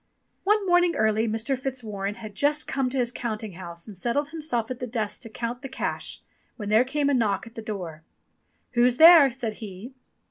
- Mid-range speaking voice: No, high, 235 Hz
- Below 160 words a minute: No, average, 200 wpm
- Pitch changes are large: No, average, 4.0 semitones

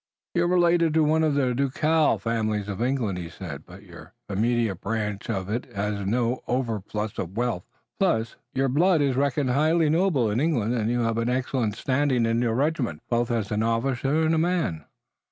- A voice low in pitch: Yes, low, 120 Hz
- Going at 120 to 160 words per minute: No, average, 190 wpm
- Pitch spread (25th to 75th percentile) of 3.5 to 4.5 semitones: No, average, 5.3 semitones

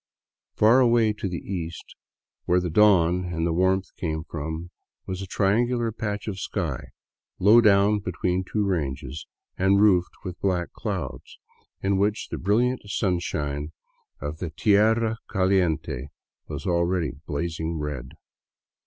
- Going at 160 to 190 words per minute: No, slow, 135 wpm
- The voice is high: No, very low, 90 Hz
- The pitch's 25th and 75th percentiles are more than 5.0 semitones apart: No, average, 4.0 semitones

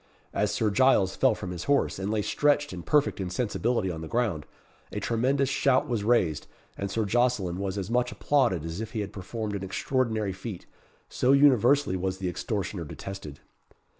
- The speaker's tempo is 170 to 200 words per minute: Yes, average, 180 wpm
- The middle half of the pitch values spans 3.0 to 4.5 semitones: No, average, 4.9 semitones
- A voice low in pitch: Yes, low, 105 Hz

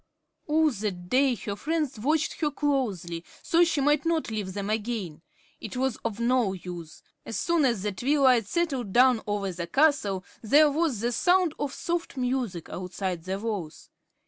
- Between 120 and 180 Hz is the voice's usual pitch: No, high, 240 Hz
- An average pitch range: No, wide, 6.9 semitones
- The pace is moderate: Yes, average, 170 wpm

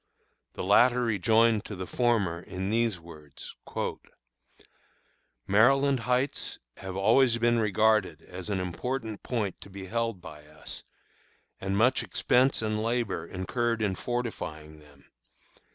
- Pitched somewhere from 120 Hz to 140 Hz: No, low, 110 Hz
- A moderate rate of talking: No, slow, 125 wpm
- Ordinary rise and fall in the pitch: Yes, average, 4.4 semitones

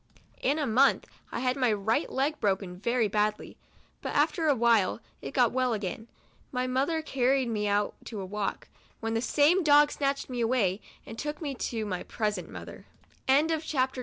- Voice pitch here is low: No, high, 235 Hz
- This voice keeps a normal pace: Yes, average, 170 wpm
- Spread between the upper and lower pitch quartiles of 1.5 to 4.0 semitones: No, average, 4.7 semitones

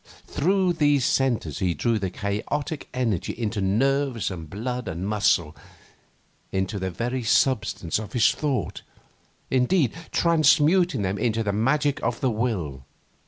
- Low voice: Yes, low, 115 Hz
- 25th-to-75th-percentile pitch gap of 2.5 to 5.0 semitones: No, wide, 5.6 semitones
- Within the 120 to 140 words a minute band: Yes, slow, 135 wpm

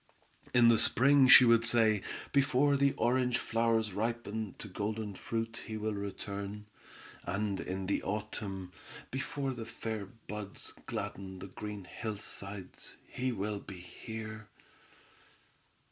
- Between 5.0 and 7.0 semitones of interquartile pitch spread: No, average, 2.7 semitones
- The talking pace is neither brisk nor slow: No, slow, 125 wpm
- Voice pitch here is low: Yes, low, 110 Hz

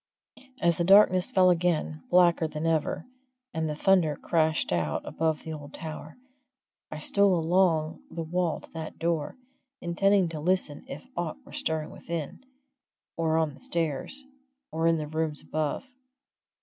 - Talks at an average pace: Yes, average, 150 wpm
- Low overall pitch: No, medium, 160 Hz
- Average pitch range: No, narrow, 2.3 semitones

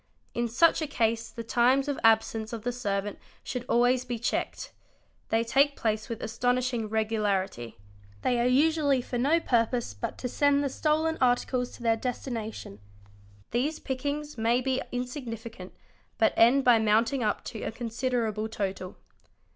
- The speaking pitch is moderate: No, high, 240 Hz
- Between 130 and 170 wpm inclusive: Yes, average, 160 wpm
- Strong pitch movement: No, average, 2.7 semitones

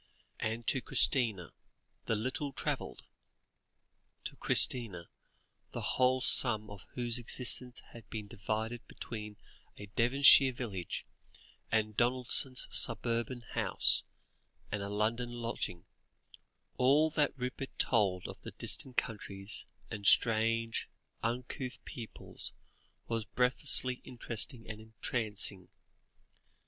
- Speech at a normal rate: No, slow, 100 wpm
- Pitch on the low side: Yes, low, 115 Hz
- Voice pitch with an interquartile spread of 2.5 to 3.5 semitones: Yes, average, 2.8 semitones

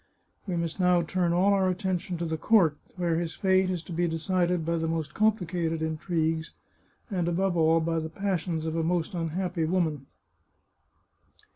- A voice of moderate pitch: Yes, medium, 170 Hz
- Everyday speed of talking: Yes, average, 170 wpm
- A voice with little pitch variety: Yes, narrow, 2.2 semitones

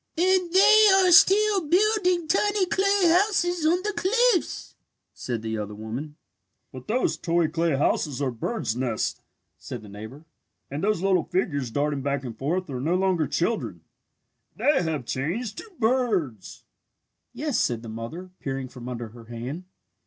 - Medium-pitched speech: Yes, medium, 175 Hz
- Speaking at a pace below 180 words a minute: Yes, average, 155 wpm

